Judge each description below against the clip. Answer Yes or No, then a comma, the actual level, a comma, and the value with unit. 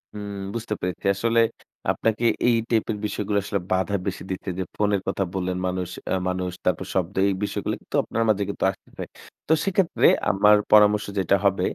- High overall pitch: No, low, 100 Hz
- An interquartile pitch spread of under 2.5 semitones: Yes, narrow, 2.1 semitones